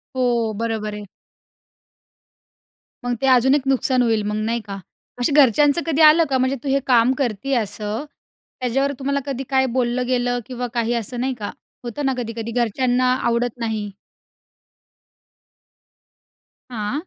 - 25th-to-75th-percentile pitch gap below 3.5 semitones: Yes, average, 2.7 semitones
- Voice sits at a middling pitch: No, high, 245 Hz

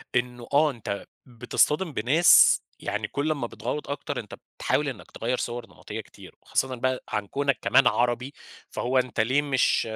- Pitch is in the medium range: No, low, 130 Hz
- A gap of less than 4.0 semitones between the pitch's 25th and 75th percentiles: Yes, average, 2.9 semitones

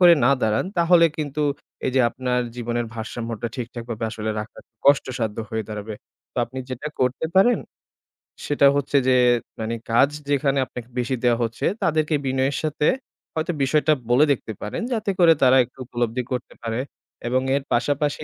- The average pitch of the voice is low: Yes, low, 130 Hz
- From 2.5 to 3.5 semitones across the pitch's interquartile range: No, average, 3.9 semitones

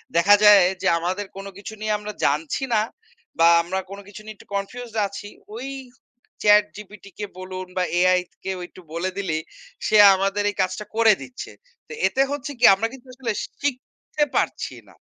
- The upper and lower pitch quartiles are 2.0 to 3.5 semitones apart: Yes, average, 3.1 semitones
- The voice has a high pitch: Yes, high, 205 Hz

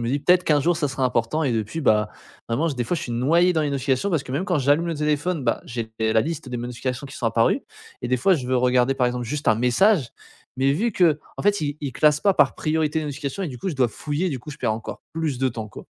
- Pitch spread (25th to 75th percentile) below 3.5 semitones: No, average, 4.4 semitones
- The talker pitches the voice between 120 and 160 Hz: Yes, medium, 140 Hz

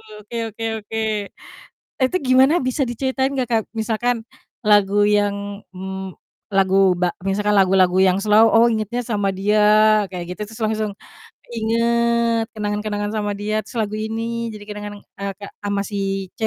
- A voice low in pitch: No, high, 210 Hz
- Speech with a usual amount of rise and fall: No, narrow, 2.3 semitones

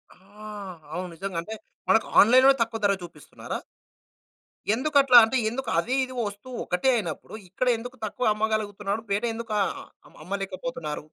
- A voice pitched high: Yes, high, 215 Hz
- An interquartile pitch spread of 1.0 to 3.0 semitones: No, average, 4.0 semitones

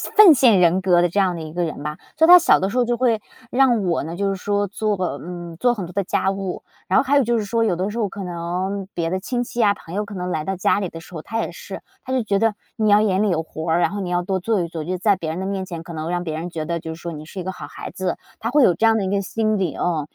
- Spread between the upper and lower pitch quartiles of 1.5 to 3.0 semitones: No, average, 4.0 semitones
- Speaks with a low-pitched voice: No, high, 190 Hz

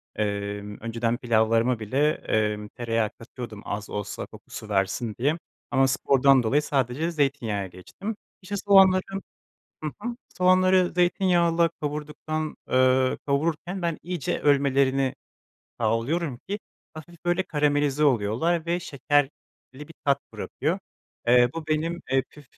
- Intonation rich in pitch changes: Yes, wide, 6.2 semitones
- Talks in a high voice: No, medium, 140 Hz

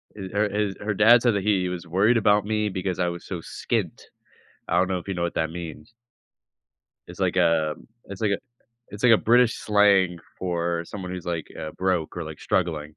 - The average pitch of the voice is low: Yes, very low, 95 Hz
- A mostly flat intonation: No, average, 3.3 semitones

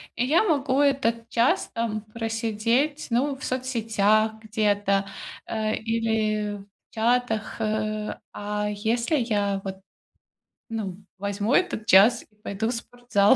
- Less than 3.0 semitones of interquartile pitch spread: Yes, narrow, 2.4 semitones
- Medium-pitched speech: No, high, 220 Hz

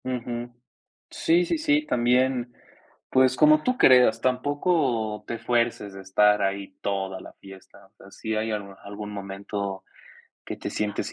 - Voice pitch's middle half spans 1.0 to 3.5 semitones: No, average, 4.3 semitones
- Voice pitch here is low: Yes, low, 110 Hz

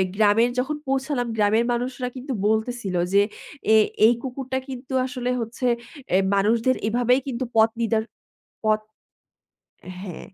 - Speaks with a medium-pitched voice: No, high, 240 Hz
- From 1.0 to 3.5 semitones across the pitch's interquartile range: Yes, average, 2.8 semitones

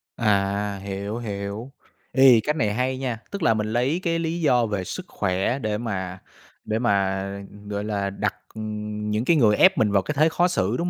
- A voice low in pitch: Yes, low, 110 Hz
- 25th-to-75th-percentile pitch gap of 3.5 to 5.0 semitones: Yes, average, 4.7 semitones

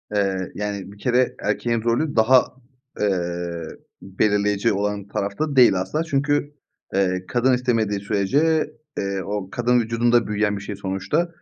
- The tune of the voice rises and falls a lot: No, average, 4.0 semitones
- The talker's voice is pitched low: Yes, low, 105 Hz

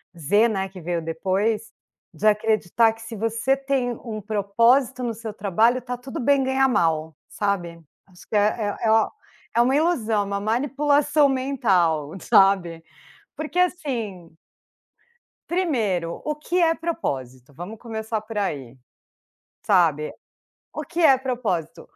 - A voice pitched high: Yes, high, 220 Hz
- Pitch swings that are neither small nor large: No, wide, 6.3 semitones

